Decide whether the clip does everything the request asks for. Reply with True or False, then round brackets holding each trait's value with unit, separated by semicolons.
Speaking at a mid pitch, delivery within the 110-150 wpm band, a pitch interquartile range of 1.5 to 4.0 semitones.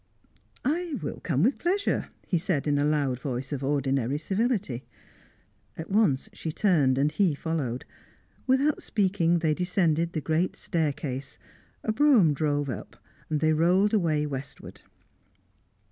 False (160 Hz; 135 wpm; 5.4 semitones)